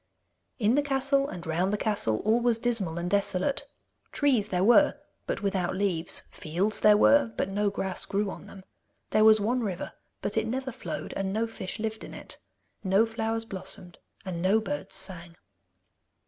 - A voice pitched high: Yes, high, 210 Hz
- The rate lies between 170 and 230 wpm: Yes, average, 175 wpm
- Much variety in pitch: No, average, 3.3 semitones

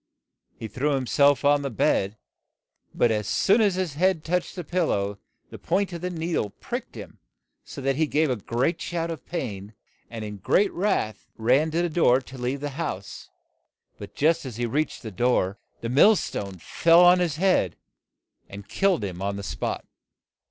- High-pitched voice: No, medium, 140 Hz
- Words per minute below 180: No, average, 190 wpm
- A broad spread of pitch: Yes, wide, 7.6 semitones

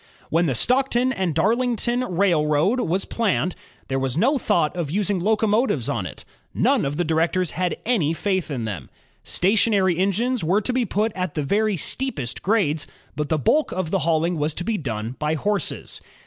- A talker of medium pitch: Yes, medium, 180 Hz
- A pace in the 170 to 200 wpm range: Yes, average, 185 wpm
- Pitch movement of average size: No, wide, 6.0 semitones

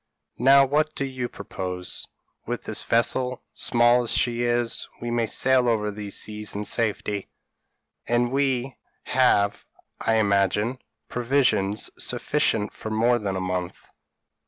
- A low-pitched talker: Yes, low, 120 Hz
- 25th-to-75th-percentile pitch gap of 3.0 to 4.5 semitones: Yes, average, 3.3 semitones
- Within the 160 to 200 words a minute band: No, slow, 135 wpm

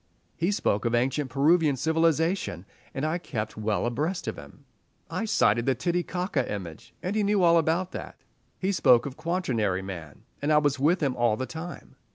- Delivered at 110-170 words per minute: No, average, 185 wpm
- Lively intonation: Yes, wide, 6.6 semitones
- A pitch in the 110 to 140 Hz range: No, medium, 150 Hz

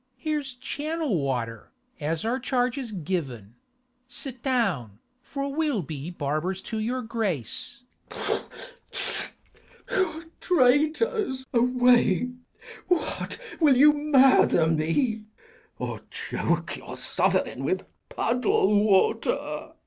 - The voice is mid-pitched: No, high, 245 Hz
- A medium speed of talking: No, slow, 105 wpm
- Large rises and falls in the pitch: Yes, wide, 8.0 semitones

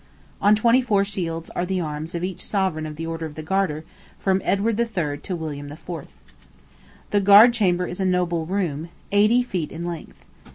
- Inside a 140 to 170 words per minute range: No, average, 190 wpm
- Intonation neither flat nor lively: Yes, average, 3.8 semitones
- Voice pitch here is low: No, medium, 180 Hz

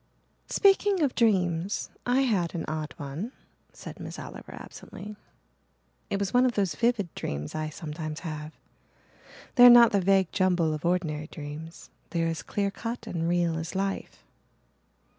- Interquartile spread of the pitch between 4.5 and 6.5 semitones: Yes, average, 5.1 semitones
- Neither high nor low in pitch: Yes, medium, 180 Hz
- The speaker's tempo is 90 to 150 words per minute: No, average, 160 wpm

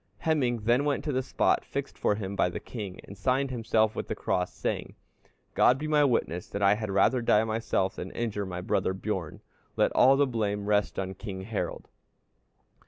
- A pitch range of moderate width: Yes, average, 4.4 semitones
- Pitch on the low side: Yes, low, 110 Hz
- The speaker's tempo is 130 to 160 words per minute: No, average, 195 wpm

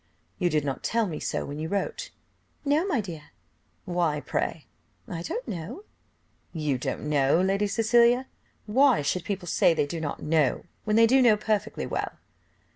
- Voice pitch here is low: No, medium, 185 Hz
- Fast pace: No, average, 170 wpm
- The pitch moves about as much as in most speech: No, wide, 6.7 semitones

